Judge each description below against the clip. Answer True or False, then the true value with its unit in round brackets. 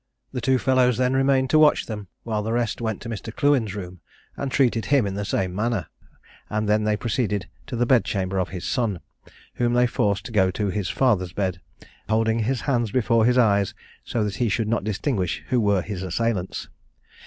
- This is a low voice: True (110 Hz)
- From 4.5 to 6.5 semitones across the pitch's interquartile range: False (3.5 semitones)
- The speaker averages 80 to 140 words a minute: False (200 wpm)